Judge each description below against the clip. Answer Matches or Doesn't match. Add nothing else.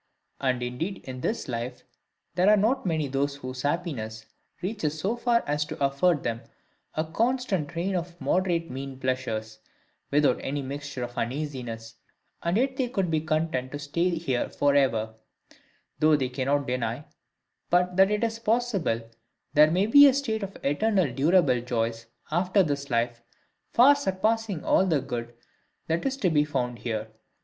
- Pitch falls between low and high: Matches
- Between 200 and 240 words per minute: Doesn't match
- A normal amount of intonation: Doesn't match